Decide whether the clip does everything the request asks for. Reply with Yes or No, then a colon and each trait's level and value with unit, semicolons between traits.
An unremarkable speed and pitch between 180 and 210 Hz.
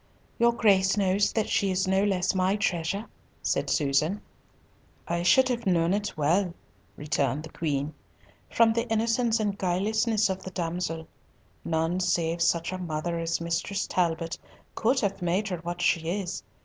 Yes: average, 160 wpm; medium, 185 Hz